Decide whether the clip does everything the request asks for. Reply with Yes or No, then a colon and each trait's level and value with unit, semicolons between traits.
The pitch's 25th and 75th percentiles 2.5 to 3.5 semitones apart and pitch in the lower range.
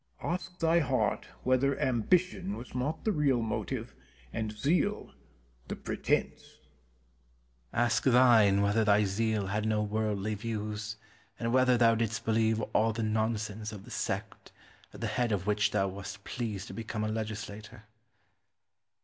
Yes: average, 2.9 semitones; low, 110 Hz